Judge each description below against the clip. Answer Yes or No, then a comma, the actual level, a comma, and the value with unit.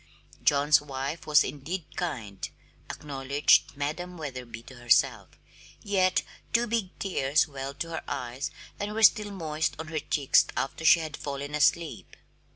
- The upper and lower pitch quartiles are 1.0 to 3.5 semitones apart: No, average, 3.9 semitones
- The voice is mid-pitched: Yes, medium, 150 Hz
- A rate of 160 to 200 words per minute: No, average, 145 wpm